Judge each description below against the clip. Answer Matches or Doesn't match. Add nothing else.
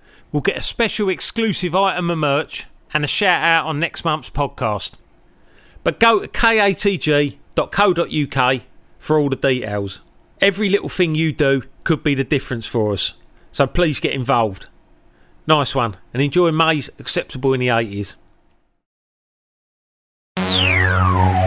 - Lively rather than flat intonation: Matches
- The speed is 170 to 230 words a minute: Doesn't match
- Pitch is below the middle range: Doesn't match